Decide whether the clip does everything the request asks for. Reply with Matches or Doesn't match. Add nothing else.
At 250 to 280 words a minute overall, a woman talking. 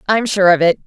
Matches